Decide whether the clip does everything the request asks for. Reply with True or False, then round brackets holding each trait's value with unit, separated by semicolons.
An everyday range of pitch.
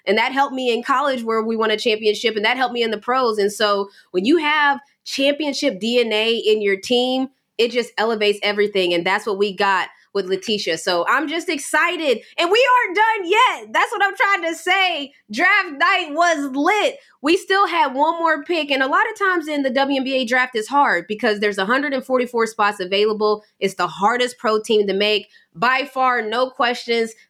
False (6.3 semitones)